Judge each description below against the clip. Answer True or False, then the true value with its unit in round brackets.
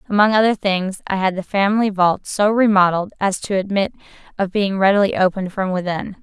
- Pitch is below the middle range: False (195 Hz)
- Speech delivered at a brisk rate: False (185 wpm)